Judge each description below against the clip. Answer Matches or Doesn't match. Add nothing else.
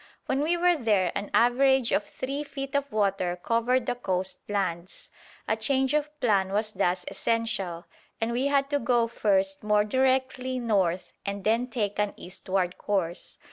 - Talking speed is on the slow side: Doesn't match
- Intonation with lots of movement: Doesn't match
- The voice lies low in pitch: Doesn't match